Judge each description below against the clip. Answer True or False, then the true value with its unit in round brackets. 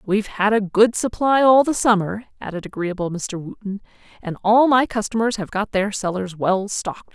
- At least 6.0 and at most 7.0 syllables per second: False (5.5 syllables/s)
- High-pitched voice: True (205 Hz)